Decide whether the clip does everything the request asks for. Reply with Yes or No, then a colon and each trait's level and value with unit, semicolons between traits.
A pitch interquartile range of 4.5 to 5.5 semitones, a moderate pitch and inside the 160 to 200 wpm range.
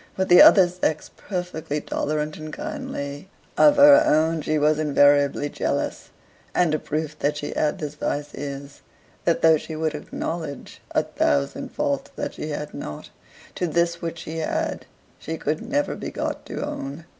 No: average, 2.7 semitones; medium, 155 Hz; average, 165 wpm